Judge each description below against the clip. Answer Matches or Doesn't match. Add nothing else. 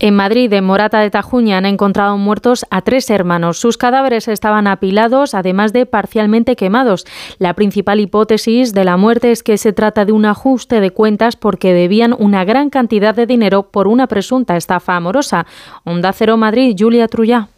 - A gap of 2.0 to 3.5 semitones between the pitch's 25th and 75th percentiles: Matches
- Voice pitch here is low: Doesn't match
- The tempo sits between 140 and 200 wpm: Matches